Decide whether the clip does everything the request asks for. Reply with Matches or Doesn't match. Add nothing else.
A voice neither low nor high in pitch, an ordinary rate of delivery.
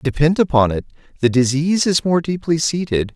Matches